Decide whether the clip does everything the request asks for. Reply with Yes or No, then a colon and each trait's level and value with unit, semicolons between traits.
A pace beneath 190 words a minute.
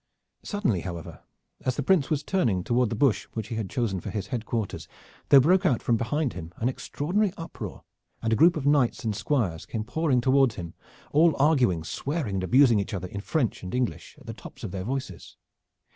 No: fast, 205 wpm